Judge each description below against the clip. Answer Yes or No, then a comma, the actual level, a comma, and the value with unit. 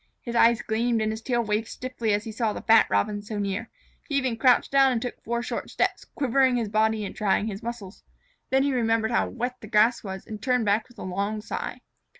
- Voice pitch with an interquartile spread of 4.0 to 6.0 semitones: No, narrow, 2.4 semitones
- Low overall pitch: No, high, 225 Hz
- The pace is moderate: No, fast, 230 wpm